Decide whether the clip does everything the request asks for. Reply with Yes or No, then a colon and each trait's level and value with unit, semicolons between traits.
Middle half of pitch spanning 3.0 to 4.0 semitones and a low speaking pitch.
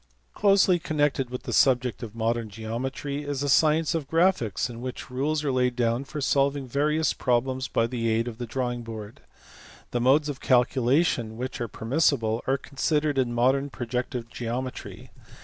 Yes: average, 3.3 semitones; low, 130 Hz